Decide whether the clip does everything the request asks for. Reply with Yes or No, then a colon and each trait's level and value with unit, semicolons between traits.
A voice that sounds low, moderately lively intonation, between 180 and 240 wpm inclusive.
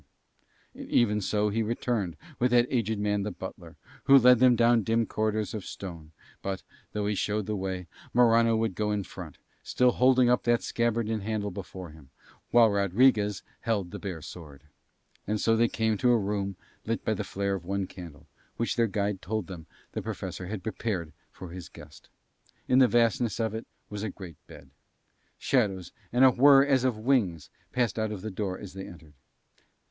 Yes: low, 105 Hz; average, 3.5 semitones; average, 190 wpm